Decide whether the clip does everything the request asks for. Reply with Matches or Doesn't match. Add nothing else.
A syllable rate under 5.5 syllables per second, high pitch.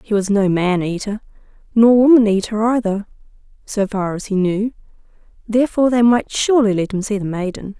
Doesn't match